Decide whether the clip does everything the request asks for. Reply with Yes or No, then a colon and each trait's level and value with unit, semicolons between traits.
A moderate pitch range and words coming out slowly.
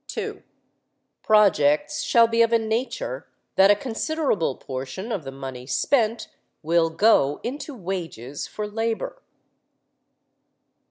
No: wide, 7.4 semitones; slow, 115 wpm